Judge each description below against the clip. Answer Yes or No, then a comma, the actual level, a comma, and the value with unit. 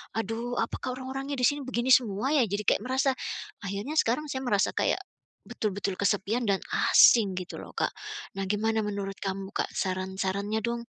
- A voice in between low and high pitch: No, high, 220 Hz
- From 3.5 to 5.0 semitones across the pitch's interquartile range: Yes, average, 4.1 semitones